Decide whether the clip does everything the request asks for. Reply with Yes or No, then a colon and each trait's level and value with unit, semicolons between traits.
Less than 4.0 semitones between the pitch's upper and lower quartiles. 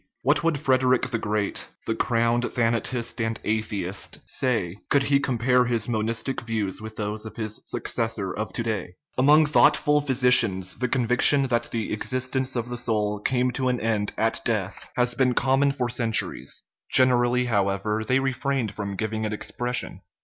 Yes: average, 2.9 semitones